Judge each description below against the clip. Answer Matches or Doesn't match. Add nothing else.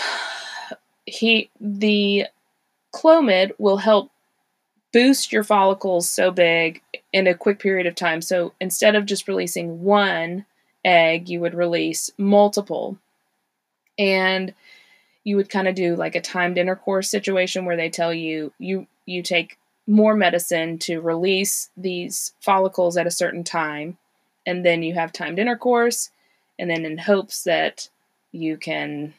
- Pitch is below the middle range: Doesn't match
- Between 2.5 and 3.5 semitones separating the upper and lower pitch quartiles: Matches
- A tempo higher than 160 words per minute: Doesn't match